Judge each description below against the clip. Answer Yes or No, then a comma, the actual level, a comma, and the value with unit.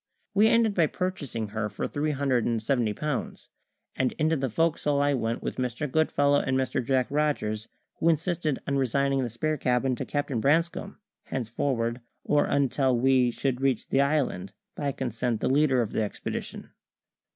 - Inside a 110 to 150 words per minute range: No, average, 170 wpm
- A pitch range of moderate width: Yes, average, 3.6 semitones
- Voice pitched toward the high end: No, low, 135 Hz